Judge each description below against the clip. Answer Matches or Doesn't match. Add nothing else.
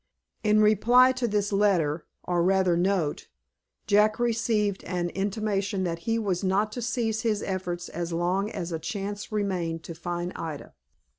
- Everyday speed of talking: Matches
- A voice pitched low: Doesn't match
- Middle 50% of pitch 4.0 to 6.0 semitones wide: Doesn't match